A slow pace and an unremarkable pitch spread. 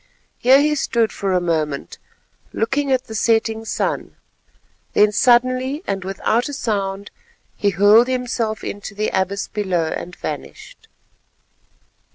Yes: slow, 130 wpm; average, 4.5 semitones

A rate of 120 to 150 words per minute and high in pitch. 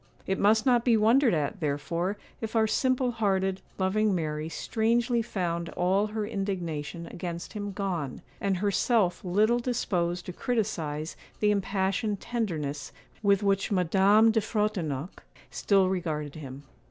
Yes: slow, 135 wpm; high, 195 Hz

